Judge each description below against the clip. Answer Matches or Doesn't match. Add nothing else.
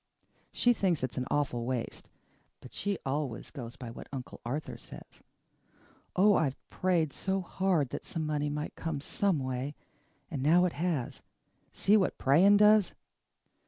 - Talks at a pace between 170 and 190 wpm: Doesn't match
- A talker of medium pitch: Matches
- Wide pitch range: Matches